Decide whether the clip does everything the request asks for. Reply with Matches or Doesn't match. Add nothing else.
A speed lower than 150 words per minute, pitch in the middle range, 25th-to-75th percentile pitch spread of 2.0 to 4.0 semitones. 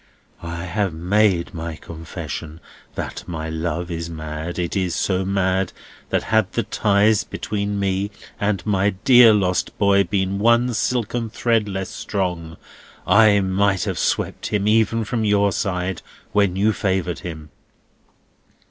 Doesn't match